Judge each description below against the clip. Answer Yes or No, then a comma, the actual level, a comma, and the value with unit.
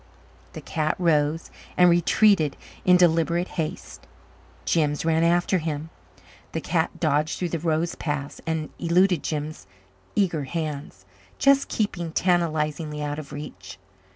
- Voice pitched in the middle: Yes, medium, 160 Hz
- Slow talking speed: Yes, slow, 125 wpm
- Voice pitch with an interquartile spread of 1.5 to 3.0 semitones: Yes, narrow, 2.6 semitones